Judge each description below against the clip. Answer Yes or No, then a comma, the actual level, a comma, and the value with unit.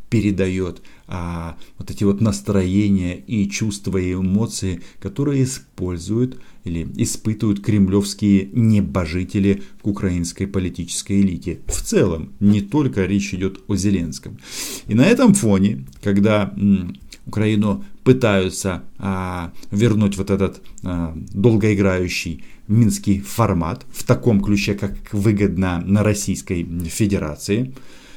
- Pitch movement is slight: Yes, narrow, 2.2 semitones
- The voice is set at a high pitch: No, low, 100 Hz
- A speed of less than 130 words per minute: Yes, slow, 110 wpm